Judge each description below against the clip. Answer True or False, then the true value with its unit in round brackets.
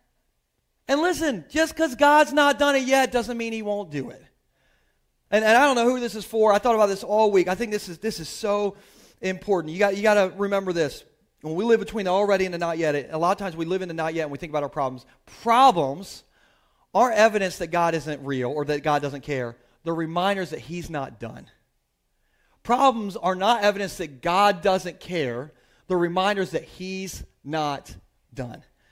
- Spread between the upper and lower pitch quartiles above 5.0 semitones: True (5.4 semitones)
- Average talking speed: False (215 wpm)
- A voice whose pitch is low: False (190 Hz)